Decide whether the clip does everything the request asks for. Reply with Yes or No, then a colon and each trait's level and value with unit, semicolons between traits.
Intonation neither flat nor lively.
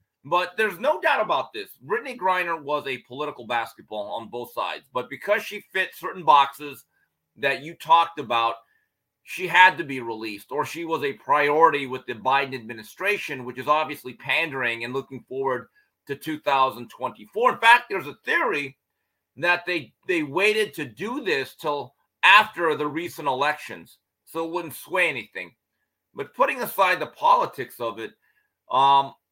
No: wide, 7.2 semitones